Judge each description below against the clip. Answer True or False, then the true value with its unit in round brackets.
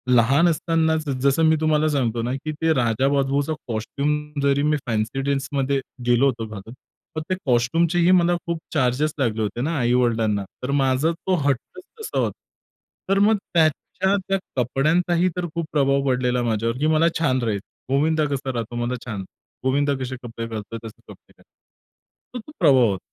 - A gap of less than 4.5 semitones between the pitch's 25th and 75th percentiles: False (4.8 semitones)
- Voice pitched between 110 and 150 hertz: True (135 Hz)